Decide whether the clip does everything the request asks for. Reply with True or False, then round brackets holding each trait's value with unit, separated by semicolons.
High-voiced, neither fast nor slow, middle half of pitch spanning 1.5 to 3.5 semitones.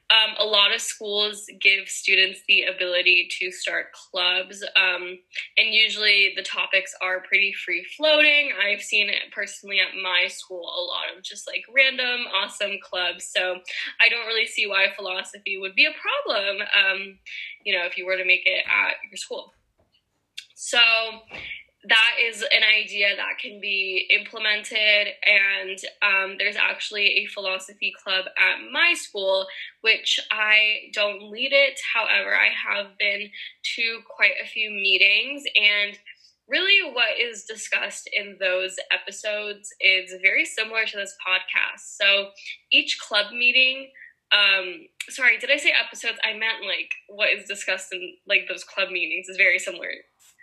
True (205 Hz; 155 wpm; 2.8 semitones)